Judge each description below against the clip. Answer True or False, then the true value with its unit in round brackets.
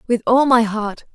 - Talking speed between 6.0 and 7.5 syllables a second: False (4.5 syllables/s)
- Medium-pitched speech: False (235 Hz)